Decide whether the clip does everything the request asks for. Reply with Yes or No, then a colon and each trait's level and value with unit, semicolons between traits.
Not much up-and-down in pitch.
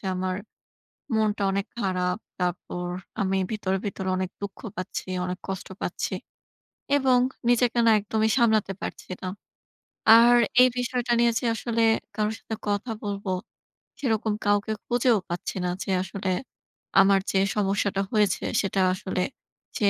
No: average, 3.1 semitones